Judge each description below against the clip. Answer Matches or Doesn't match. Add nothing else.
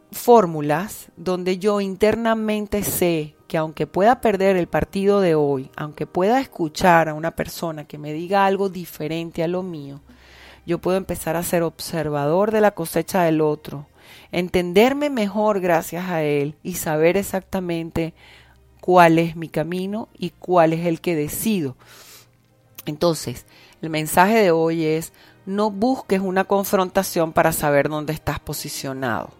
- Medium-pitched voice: Matches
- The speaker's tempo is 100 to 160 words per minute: Matches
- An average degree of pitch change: Matches